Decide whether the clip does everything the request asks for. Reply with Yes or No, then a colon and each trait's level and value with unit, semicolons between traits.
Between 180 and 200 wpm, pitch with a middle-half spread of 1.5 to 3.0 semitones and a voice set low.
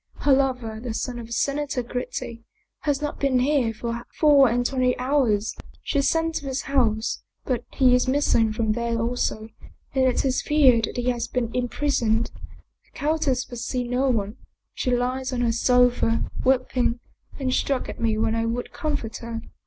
No: average, 185 wpm; narrow, 2.5 semitones; very high, 250 Hz